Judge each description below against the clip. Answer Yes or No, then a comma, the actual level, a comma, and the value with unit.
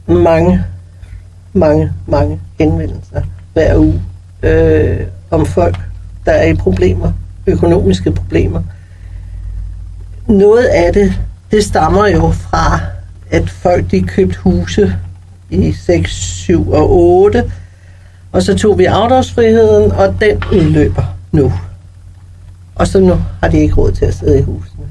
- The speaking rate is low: Yes, slow, 130 wpm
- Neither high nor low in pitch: No, very low, 90 Hz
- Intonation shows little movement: Yes, narrow, 1.1 semitones